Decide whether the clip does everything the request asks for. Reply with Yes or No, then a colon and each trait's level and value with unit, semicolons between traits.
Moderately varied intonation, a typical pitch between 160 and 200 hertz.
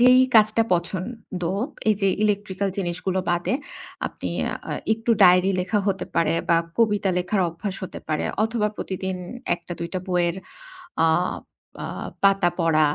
Yes: average, 3.1 semitones; high, 190 Hz